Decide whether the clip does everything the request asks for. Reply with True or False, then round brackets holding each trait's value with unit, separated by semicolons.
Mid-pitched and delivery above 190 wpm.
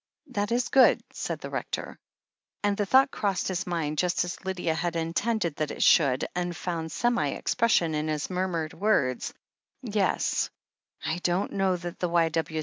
False (175 Hz; 170 wpm)